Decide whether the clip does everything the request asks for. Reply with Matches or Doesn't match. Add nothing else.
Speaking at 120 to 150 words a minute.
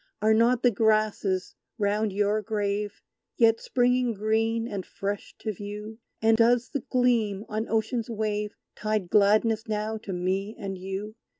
Matches